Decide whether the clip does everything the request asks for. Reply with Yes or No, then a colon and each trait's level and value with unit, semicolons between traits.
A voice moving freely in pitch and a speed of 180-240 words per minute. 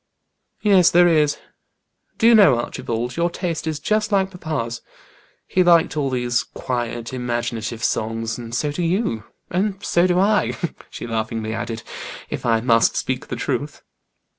No: wide, 7.2 semitones; average, 155 wpm